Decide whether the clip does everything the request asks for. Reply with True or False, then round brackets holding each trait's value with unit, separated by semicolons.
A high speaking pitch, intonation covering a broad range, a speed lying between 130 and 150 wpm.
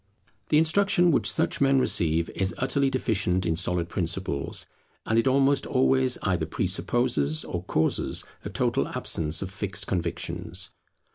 False (95 Hz; 7.7 semitones; 140 wpm)